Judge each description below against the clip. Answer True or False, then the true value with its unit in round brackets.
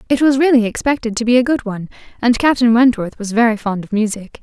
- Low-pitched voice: False (235 Hz)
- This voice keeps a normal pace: False (230 wpm)